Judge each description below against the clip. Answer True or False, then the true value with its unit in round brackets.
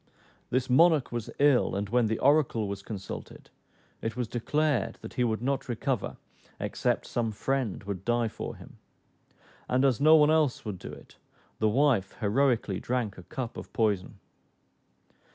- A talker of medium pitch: False (120 Hz)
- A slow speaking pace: False (160 wpm)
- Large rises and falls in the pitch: False (4.2 semitones)